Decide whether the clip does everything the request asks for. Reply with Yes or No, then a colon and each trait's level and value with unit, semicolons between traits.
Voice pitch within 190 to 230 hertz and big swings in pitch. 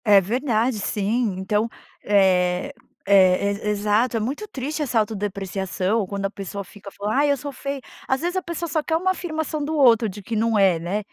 Yes: high, 215 Hz; wide, 5.8 semitones